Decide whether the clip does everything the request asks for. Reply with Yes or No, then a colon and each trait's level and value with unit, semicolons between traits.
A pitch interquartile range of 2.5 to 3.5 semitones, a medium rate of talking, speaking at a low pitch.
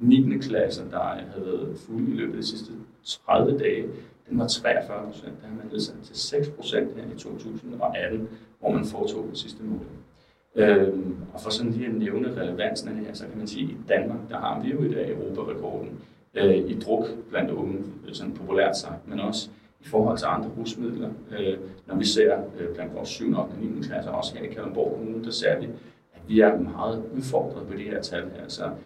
Yes: average, 3.1 semitones; average, 210 wpm; low, 110 Hz